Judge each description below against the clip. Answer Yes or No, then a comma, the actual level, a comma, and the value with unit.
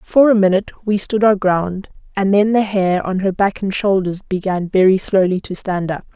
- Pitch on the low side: No, high, 195 Hz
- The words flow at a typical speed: No, fast, 215 wpm